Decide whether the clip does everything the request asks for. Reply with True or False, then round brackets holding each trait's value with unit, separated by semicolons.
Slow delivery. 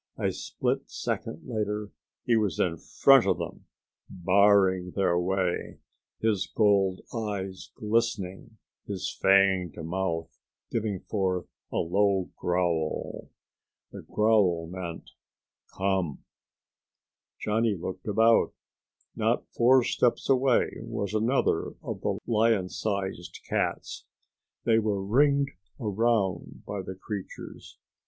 True (105 wpm)